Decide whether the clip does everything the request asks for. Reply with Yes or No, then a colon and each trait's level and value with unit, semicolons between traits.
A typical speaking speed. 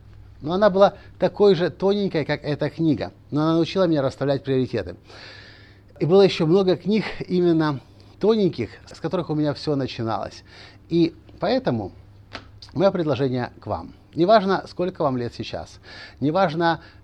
Yes: average, 140 wpm